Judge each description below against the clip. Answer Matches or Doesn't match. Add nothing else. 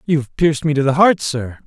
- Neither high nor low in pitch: Matches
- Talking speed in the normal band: Doesn't match